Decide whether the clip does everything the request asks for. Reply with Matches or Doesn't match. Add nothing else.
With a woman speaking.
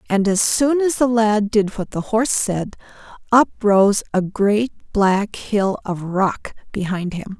Matches